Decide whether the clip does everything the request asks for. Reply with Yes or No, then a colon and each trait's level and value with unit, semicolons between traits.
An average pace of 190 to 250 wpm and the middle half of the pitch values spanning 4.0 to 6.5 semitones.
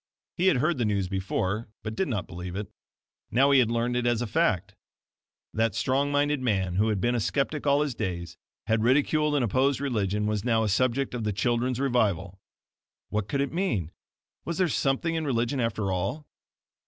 Yes: average, 195 wpm; average, 5.1 semitones